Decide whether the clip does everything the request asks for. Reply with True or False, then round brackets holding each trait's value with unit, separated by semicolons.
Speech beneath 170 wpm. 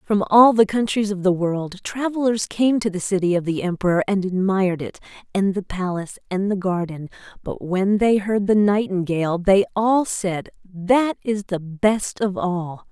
False (180 wpm)